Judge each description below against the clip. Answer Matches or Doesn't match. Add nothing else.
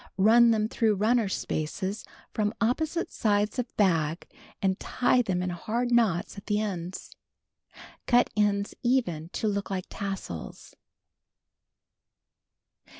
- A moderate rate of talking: Doesn't match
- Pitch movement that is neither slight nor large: Matches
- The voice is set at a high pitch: Matches